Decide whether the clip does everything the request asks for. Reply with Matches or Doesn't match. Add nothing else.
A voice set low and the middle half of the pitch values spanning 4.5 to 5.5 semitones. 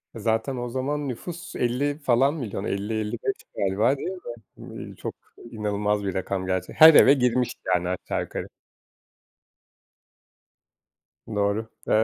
Matches